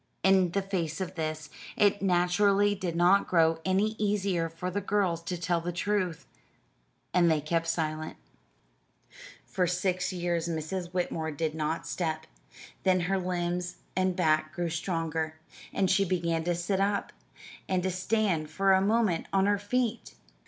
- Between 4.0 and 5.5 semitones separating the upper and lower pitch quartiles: No, average, 2.8 semitones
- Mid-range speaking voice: Yes, medium, 180 Hz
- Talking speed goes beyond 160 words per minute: No, average, 155 wpm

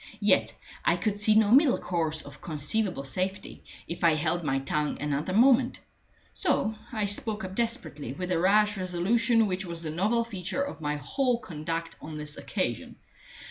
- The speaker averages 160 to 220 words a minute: Yes, average, 170 wpm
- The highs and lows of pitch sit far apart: Yes, wide, 6.0 semitones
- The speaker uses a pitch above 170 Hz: Yes, medium, 185 Hz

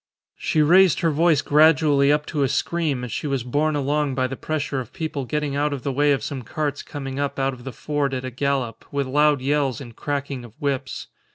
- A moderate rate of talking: No, fast, 225 wpm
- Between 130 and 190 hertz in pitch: Yes, medium, 140 Hz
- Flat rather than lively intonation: Yes, narrow, 2.1 semitones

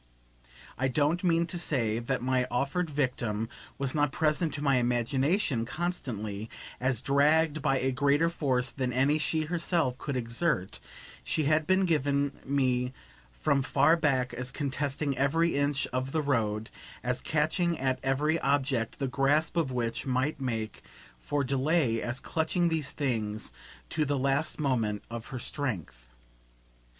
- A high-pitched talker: No, low, 135 Hz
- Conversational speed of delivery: Yes, average, 150 wpm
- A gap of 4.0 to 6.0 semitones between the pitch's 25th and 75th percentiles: No, average, 3.5 semitones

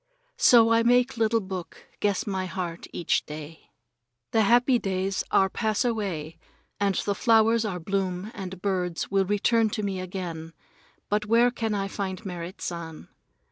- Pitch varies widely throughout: No, average, 3.5 semitones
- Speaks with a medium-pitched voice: No, high, 195 Hz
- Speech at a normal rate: Yes, average, 155 wpm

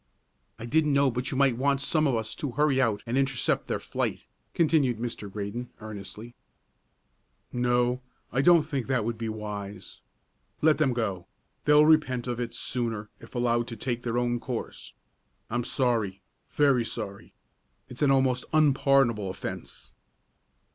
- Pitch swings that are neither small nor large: Yes, average, 3.4 semitones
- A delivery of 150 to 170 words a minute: Yes, average, 155 wpm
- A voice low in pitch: Yes, low, 120 Hz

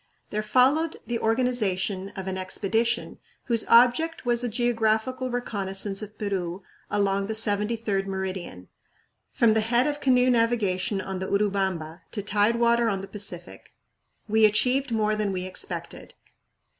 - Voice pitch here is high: Yes, high, 215 Hz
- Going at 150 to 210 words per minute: No, average, 140 wpm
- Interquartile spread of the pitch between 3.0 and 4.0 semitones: Yes, average, 3.5 semitones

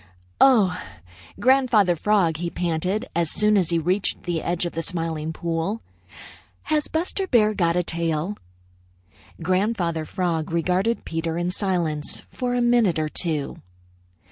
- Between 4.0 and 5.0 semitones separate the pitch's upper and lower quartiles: Yes, average, 4.4 semitones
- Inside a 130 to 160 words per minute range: Yes, average, 140 wpm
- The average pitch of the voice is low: No, medium, 175 Hz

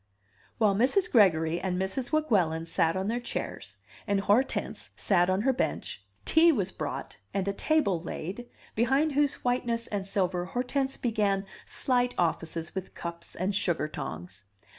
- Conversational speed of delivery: Yes, average, 150 wpm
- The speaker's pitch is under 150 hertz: No, high, 200 Hz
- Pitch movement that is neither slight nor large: No, wide, 5.7 semitones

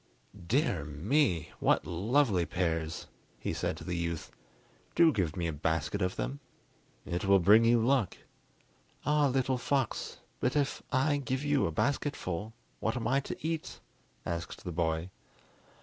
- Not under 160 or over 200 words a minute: No, average, 150 wpm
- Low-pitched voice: Yes, low, 105 Hz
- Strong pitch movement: Yes, wide, 8.3 semitones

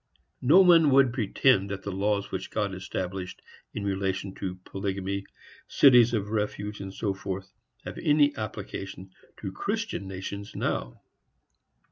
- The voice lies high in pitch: No, low, 100 Hz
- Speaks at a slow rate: Yes, slow, 125 wpm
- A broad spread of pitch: No, average, 4.1 semitones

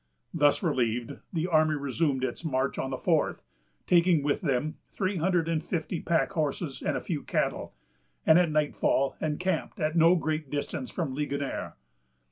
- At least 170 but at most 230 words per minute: No, average, 160 wpm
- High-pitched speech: No, medium, 155 Hz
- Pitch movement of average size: Yes, average, 3.1 semitones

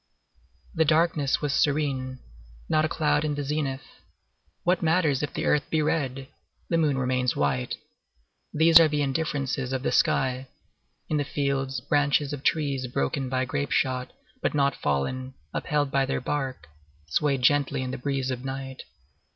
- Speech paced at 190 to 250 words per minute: No, average, 165 wpm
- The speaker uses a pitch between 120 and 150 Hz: Yes, medium, 140 Hz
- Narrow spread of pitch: Yes, narrow, 2.3 semitones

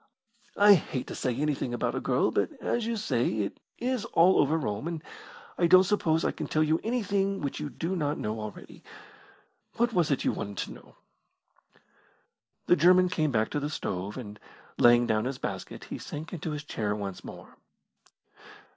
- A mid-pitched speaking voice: Yes, medium, 150 Hz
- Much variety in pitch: Yes, wide, 7.4 semitones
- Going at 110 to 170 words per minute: No, average, 180 wpm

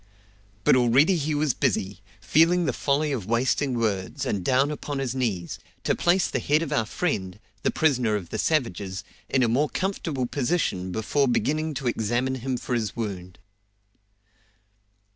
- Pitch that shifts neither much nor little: No, wide, 5.7 semitones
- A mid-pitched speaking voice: No, low, 130 Hz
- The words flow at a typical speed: Yes, average, 160 wpm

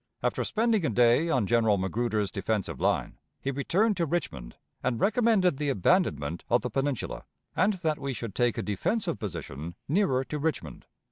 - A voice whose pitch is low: Yes, low, 130 Hz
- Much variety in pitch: Yes, wide, 8.2 semitones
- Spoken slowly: No, average, 165 wpm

